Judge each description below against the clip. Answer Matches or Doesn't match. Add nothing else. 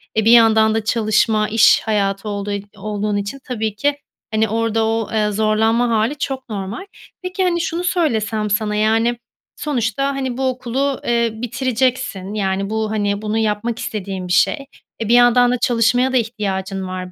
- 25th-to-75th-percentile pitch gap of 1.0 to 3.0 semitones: Matches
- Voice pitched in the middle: Doesn't match